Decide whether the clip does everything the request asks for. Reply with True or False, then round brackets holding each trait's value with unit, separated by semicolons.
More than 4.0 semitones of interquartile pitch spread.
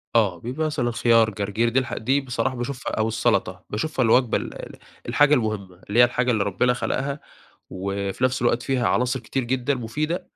False (3.2 semitones)